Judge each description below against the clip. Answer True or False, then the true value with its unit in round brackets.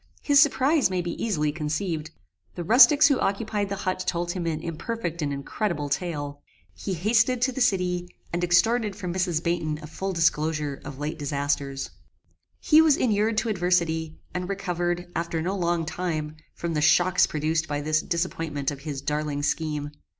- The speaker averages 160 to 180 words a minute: True (170 wpm)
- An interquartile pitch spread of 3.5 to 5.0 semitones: True (4.3 semitones)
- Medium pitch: True (170 Hz)